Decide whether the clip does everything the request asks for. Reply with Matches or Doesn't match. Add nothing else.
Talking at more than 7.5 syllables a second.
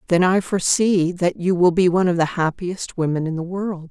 Doesn't match